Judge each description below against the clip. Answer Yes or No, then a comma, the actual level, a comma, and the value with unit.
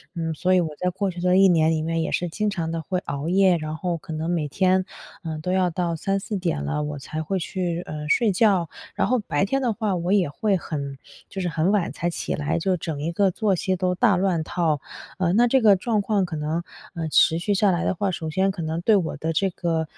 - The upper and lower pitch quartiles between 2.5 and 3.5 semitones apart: Yes, average, 3.2 semitones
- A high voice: No, medium, 175 Hz